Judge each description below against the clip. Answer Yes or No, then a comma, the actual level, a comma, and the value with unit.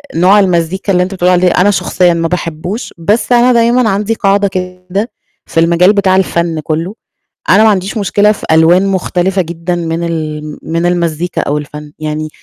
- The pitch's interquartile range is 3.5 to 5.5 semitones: No, average, 3.1 semitones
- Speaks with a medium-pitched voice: Yes, medium, 180 Hz